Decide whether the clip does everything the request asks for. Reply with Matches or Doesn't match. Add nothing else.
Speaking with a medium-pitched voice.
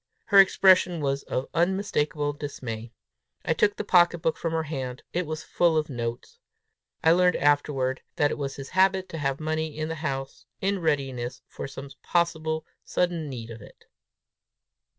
Matches